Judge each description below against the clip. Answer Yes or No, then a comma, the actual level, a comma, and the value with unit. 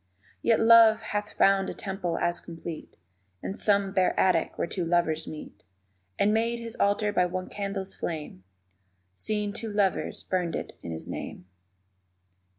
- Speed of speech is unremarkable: Yes, average, 155 wpm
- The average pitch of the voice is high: Yes, high, 195 Hz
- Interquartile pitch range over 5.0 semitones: No, average, 3.3 semitones